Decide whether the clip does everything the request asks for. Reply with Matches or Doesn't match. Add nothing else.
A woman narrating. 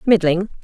Matches